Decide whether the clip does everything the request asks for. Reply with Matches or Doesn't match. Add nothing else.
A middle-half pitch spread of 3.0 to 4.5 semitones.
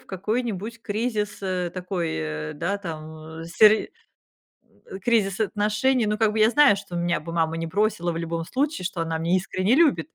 Matches